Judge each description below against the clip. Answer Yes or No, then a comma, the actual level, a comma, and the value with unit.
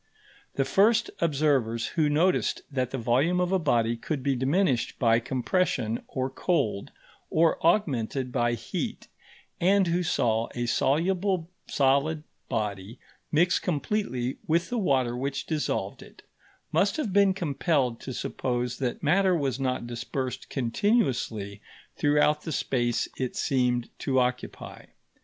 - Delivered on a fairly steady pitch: No, wide, 5.6 semitones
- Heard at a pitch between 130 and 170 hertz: Yes, low, 135 Hz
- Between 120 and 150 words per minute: Yes, slow, 135 wpm